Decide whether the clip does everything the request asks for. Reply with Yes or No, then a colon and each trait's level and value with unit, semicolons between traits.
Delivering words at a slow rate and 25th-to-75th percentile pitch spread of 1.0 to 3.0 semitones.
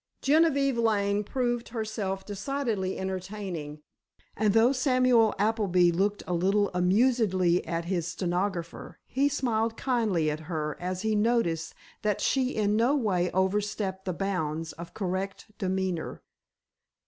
No: slow, 125 wpm; average, 4.0 semitones